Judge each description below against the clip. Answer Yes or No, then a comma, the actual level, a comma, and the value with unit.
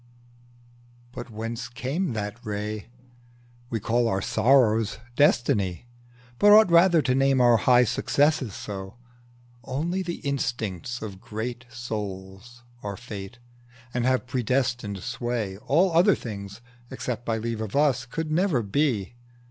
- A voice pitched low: Yes, low, 120 Hz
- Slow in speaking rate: Yes, slow, 130 wpm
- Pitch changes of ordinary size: Yes, average, 4.2 semitones